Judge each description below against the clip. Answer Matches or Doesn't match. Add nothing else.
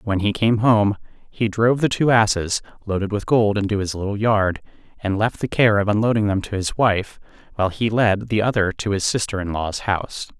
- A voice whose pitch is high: Doesn't match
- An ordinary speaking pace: Doesn't match